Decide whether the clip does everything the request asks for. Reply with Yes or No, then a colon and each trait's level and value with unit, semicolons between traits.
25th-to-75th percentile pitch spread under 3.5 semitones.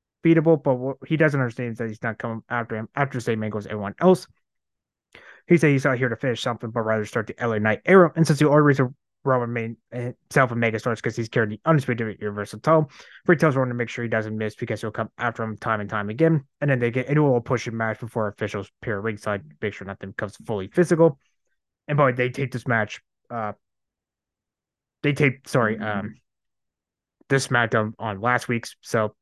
No: average, 3.8 semitones